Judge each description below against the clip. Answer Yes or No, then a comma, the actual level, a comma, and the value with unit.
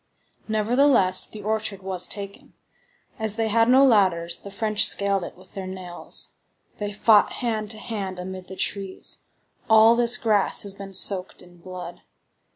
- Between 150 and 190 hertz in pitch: No, high, 200 Hz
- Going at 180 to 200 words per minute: No, average, 160 wpm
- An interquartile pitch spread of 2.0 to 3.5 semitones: Yes, average, 2.7 semitones